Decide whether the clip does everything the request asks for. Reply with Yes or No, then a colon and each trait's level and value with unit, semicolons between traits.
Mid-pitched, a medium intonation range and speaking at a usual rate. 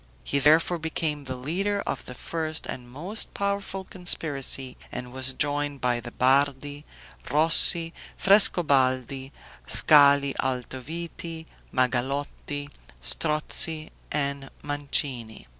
No: medium, 145 Hz; average, 3.6 semitones; slow, 100 wpm